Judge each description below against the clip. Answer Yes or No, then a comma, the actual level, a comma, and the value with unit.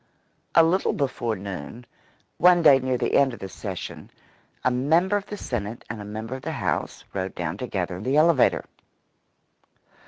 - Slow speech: No, average, 175 wpm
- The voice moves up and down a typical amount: No, wide, 6.9 semitones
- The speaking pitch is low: Yes, low, 125 Hz